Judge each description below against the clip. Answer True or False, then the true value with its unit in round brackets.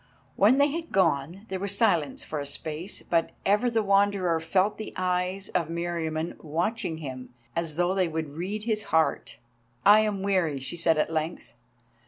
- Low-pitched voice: False (180 Hz)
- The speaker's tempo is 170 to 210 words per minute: True (175 wpm)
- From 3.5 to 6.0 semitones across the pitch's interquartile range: True (3.8 semitones)